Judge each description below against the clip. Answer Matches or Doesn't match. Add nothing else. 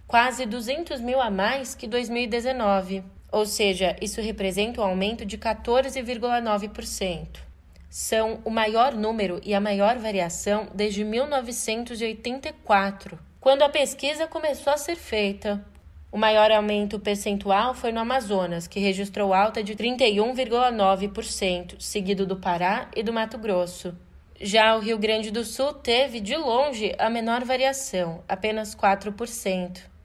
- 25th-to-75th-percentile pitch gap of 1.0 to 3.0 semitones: Doesn't match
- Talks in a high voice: Matches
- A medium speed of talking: Matches